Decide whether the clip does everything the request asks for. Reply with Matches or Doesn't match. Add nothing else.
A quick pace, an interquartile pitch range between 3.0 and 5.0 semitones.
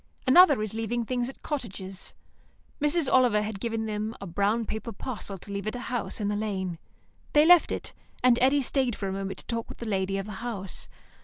Matches